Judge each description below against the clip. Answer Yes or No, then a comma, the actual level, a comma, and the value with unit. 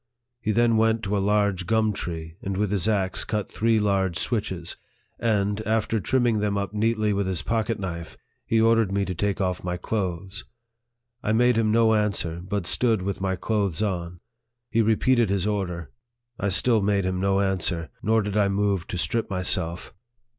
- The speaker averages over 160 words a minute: Yes, average, 185 wpm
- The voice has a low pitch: Yes, low, 100 Hz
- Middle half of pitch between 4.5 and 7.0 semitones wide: No, average, 2.8 semitones